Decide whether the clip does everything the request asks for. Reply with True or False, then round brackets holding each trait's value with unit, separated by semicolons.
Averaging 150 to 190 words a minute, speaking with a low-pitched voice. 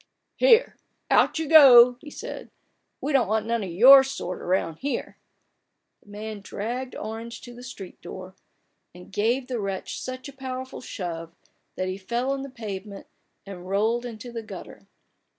False (180 wpm; 230 Hz)